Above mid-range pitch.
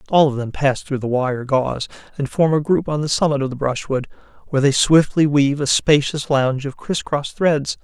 No: medium, 140 Hz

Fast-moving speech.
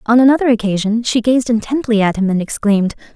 No: average, 190 wpm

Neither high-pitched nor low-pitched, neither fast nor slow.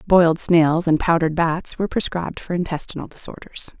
Yes: medium, 165 Hz; average, 160 wpm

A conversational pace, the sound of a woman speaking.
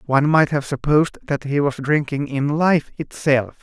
No: average, 180 wpm; male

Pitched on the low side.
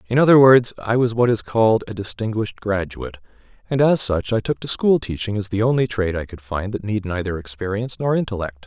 Yes: low, 110 Hz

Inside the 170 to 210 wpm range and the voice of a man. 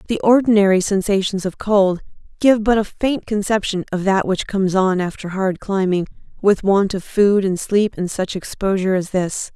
No: average, 180 wpm; female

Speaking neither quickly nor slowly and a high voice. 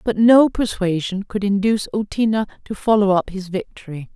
Yes: average, 160 wpm; high, 205 Hz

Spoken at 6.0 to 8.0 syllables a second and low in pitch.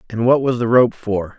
No: 5.0 syllables/s; low, 115 Hz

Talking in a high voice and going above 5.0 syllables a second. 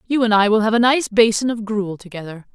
Yes: high, 215 Hz; 5.8 syllables/s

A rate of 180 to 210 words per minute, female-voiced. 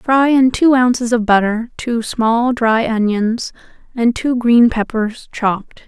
No: average, 155 wpm; female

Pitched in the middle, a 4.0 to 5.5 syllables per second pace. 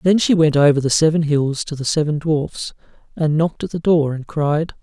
Yes: medium, 155 Hz; 5.2 syllables/s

